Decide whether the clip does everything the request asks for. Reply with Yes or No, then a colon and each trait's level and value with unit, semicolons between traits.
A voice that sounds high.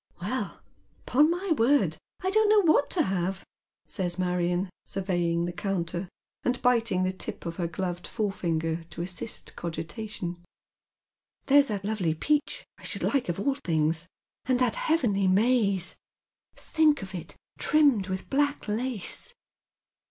Yes: high, 195 Hz